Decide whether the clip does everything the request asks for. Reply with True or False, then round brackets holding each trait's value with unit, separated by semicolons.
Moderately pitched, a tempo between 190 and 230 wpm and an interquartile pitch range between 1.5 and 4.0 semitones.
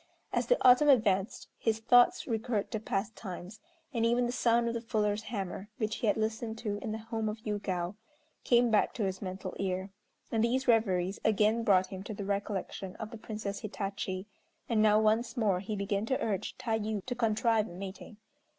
False (215 Hz; 195 wpm; 2.5 semitones)